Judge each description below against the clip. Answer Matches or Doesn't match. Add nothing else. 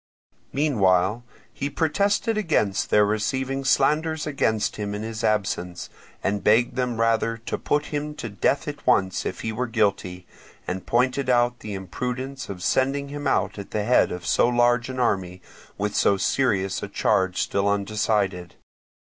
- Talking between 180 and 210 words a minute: Doesn't match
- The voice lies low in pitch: Matches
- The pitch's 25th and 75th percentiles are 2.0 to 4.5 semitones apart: Doesn't match